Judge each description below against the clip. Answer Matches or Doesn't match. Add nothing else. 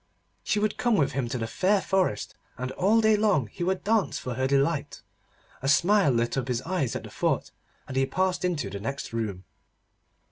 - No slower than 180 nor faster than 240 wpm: Matches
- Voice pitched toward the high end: Doesn't match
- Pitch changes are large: Matches